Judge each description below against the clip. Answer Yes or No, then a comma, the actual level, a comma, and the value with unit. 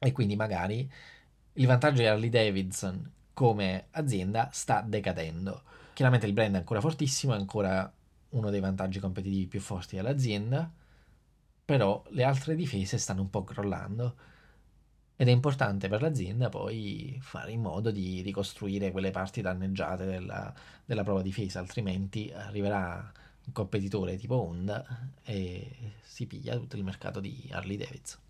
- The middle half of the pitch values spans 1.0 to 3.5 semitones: No, average, 4.4 semitones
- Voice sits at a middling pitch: No, low, 105 Hz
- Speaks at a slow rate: No, average, 145 wpm